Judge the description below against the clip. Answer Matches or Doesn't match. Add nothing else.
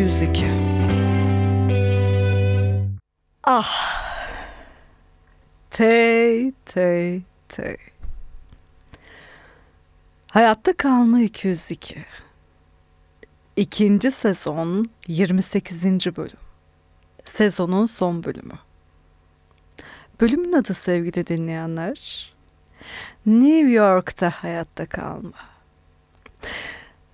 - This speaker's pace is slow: Matches